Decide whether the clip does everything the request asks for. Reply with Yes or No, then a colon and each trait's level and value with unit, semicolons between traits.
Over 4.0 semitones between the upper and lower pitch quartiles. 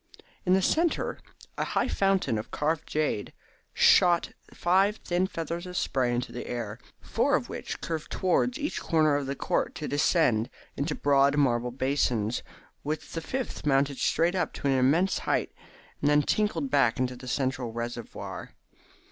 Yes: average, 5.3 semitones